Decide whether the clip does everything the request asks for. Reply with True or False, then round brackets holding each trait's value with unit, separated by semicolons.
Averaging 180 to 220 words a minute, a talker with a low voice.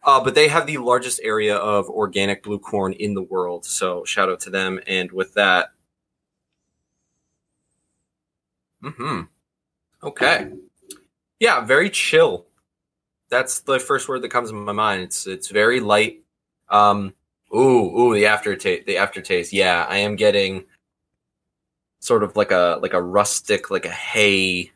False (150 wpm; 105 Hz)